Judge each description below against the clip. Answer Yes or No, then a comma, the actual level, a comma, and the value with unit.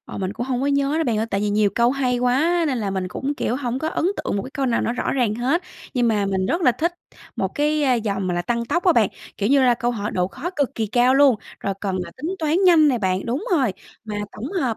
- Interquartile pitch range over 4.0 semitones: Yes, average, 5.2 semitones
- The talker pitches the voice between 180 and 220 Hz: No, high, 245 Hz